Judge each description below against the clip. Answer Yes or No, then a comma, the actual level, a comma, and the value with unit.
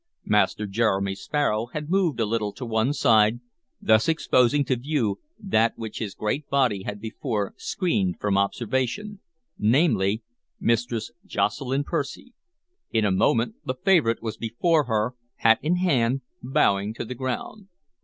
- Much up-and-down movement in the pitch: No, average, 4.8 semitones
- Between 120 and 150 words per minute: Yes, average, 145 wpm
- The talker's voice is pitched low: Yes, low, 115 Hz